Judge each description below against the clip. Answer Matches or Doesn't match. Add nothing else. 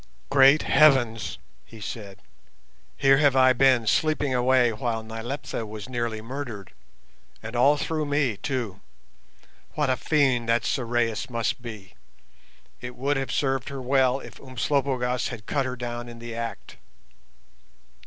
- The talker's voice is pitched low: Matches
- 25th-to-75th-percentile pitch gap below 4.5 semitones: Matches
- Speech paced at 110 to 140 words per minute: Matches